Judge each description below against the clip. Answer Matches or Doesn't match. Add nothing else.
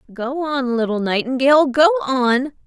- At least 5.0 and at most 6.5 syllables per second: Doesn't match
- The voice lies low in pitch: Doesn't match